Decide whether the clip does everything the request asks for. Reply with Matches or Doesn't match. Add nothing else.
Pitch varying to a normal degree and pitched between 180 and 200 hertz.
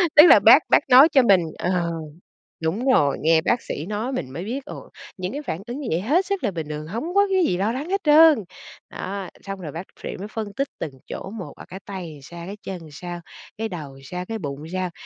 Doesn't match